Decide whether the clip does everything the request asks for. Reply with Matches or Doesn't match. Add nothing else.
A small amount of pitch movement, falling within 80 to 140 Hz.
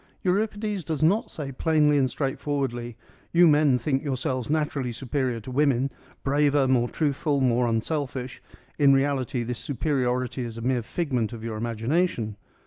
Doesn't match